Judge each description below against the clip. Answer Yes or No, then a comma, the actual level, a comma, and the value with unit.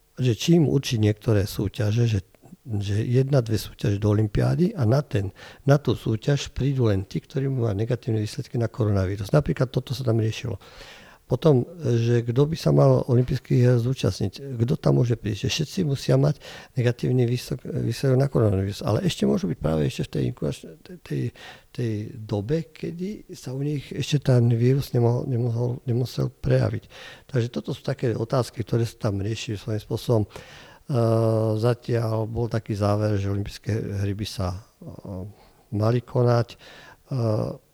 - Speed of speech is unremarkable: Yes, average, 155 wpm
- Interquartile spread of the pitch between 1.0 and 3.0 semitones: No, average, 3.7 semitones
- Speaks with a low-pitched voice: Yes, low, 120 Hz